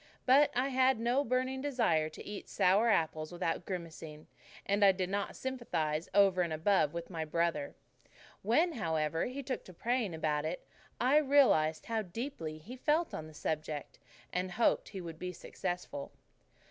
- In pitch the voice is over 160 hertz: Yes, medium, 185 Hz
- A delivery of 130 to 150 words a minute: No, average, 165 wpm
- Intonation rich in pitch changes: Yes, wide, 7.6 semitones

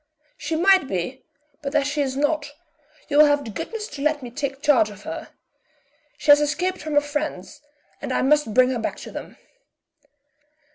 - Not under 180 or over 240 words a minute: Yes, average, 190 wpm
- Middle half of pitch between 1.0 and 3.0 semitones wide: Yes, narrow, 2.4 semitones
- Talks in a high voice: Yes, very high, 290 Hz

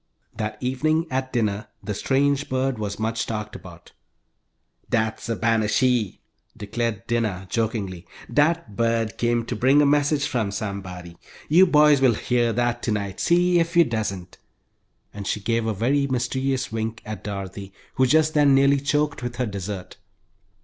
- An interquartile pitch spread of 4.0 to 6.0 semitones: Yes, average, 4.5 semitones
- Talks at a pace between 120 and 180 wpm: Yes, average, 155 wpm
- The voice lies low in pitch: Yes, low, 115 Hz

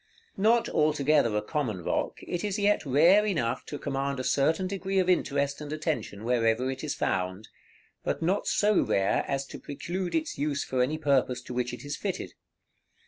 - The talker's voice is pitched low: No, medium, 145 Hz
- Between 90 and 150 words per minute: No, average, 185 wpm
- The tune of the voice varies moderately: No, wide, 5.7 semitones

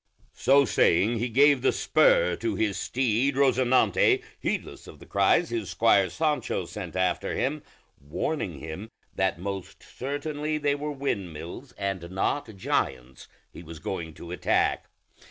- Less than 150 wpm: Yes, average, 140 wpm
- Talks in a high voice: No, low, 115 Hz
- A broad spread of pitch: Yes, wide, 7.4 semitones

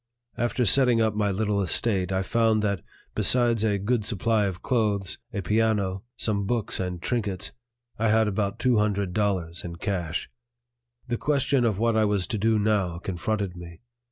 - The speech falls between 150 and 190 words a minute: Yes, average, 170 wpm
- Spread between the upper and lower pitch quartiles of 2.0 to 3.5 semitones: Yes, average, 2.9 semitones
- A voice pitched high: No, low, 105 Hz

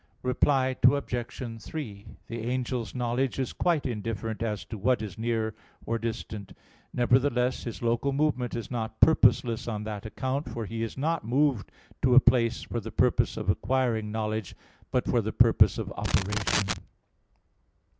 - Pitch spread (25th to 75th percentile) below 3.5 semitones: Yes, average, 2.8 semitones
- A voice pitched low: Yes, low, 115 Hz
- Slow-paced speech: No, average, 155 wpm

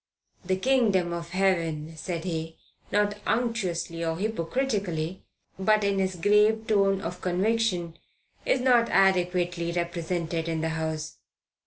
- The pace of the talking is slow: Yes, slow, 125 wpm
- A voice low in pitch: No, medium, 180 Hz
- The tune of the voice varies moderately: Yes, average, 3.8 semitones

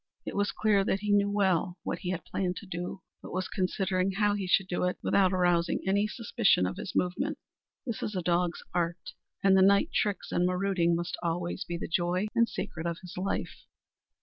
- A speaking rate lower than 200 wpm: No, fast, 205 wpm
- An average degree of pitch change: No, narrow, 2.2 semitones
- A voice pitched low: No, medium, 185 Hz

